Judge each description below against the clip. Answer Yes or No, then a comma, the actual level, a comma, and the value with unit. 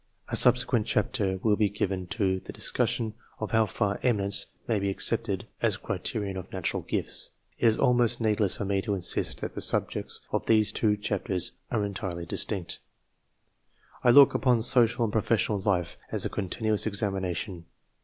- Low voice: Yes, low, 105 Hz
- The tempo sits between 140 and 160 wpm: No, average, 175 wpm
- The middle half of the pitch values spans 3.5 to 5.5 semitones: No, average, 2.7 semitones